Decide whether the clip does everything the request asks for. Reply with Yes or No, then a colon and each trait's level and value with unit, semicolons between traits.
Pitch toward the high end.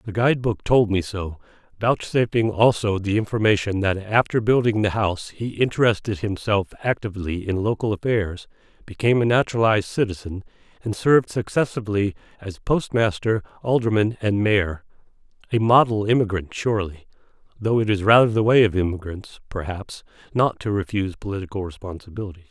No: low, 105 Hz